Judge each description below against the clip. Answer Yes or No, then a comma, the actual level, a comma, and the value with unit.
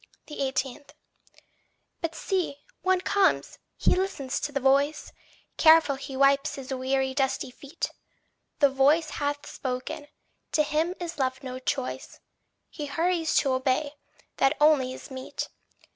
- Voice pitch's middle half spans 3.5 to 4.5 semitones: No, average, 2.8 semitones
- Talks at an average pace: No, slow, 130 wpm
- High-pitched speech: Yes, very high, 280 Hz